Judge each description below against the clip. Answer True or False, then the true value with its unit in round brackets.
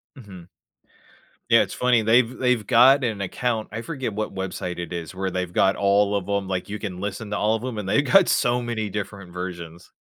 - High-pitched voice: False (105 Hz)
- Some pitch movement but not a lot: True (4.0 semitones)